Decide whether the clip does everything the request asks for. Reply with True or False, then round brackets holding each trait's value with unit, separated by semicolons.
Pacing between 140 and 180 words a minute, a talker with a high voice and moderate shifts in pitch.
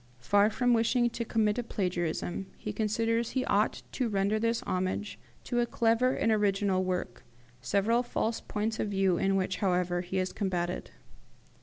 True (165 wpm; 205 Hz; 3.5 semitones)